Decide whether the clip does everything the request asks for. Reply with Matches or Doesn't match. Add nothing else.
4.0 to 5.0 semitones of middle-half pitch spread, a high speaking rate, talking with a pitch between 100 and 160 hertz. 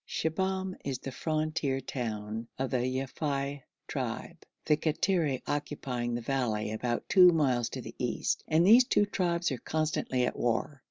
Doesn't match